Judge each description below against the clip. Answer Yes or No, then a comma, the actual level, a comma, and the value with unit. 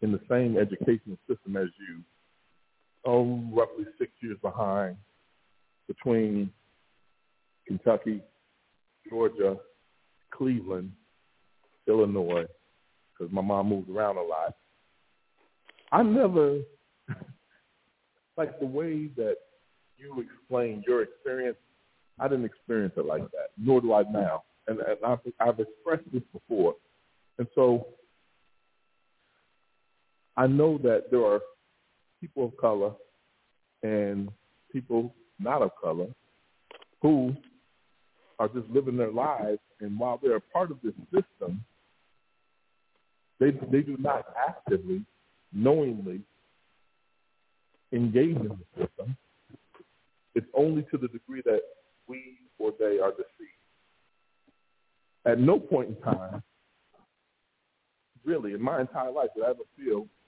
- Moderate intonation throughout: No, wide, 7.0 semitones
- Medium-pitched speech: No, low, 125 Hz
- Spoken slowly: Yes, slow, 115 wpm